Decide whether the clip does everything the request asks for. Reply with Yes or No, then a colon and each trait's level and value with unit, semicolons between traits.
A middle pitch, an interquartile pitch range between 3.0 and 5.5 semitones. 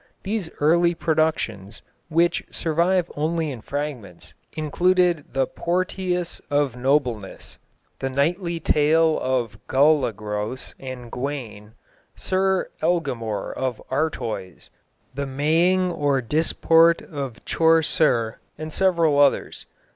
Yes: medium, 150 Hz; average, 4.7 semitones